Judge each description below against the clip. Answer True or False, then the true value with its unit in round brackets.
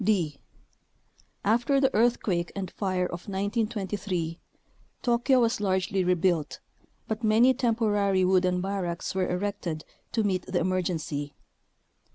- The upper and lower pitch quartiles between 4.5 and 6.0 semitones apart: False (3.4 semitones)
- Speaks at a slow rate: True (115 wpm)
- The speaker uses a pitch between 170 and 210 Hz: True (190 Hz)